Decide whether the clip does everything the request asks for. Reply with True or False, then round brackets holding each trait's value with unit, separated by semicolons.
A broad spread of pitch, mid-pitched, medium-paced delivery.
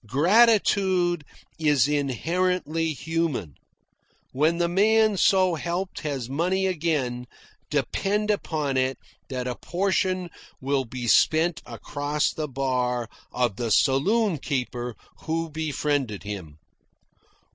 False (5.7 semitones; 155 Hz; 105 wpm)